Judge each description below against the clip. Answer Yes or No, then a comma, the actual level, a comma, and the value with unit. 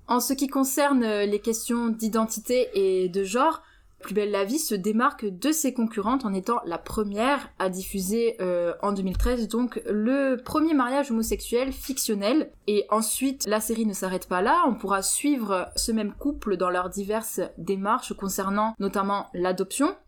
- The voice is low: No, high, 220 Hz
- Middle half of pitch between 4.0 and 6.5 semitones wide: Yes, average, 4.7 semitones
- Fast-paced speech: No, average, 165 wpm